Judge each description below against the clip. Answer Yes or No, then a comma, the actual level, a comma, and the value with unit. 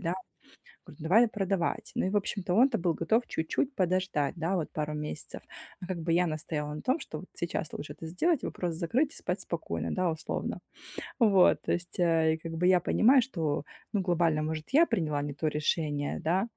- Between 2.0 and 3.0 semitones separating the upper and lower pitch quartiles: No, average, 3.6 semitones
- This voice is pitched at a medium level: Yes, medium, 175 Hz